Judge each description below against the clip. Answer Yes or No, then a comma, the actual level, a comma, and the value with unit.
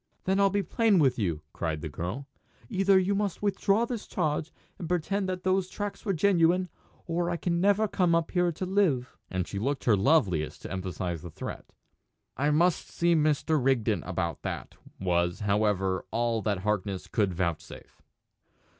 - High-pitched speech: No, medium, 150 Hz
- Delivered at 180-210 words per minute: No, average, 170 wpm